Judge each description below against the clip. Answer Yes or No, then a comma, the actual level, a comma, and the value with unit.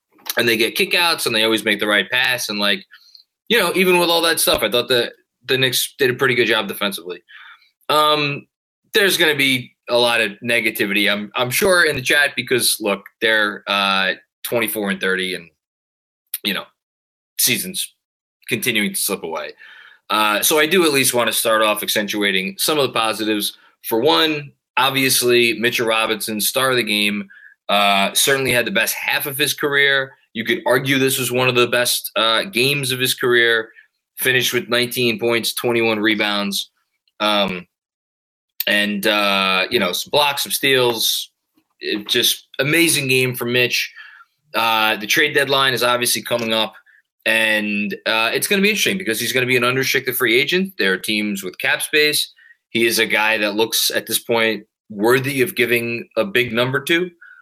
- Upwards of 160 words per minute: Yes, average, 185 wpm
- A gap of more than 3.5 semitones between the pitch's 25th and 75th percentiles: Yes, average, 4.1 semitones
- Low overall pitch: Yes, low, 120 Hz